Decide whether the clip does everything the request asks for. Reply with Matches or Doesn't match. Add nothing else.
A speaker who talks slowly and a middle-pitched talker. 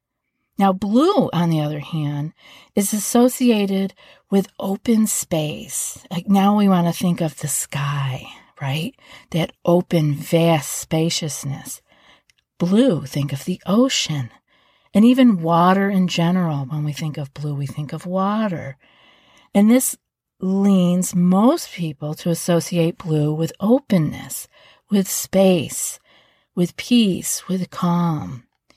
Matches